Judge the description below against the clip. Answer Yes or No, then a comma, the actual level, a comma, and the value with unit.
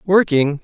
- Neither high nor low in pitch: Yes, medium, 165 Hz